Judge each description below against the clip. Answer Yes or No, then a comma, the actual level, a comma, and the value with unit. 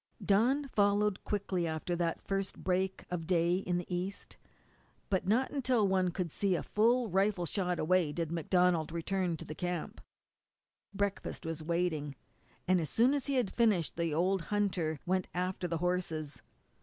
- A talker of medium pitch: Yes, medium, 180 Hz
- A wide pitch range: No, average, 3.0 semitones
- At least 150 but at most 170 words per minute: Yes, average, 165 wpm